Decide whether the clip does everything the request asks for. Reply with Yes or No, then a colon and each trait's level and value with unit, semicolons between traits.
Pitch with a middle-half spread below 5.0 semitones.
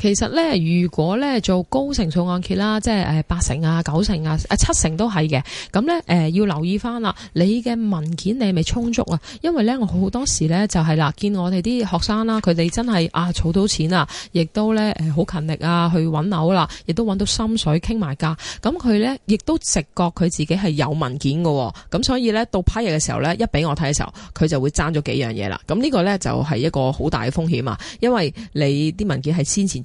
No: wide, 5.5 semitones